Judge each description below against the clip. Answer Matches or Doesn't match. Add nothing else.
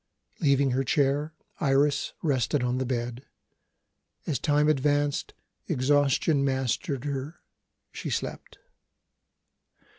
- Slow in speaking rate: Matches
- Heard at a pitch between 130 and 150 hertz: Matches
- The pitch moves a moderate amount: Doesn't match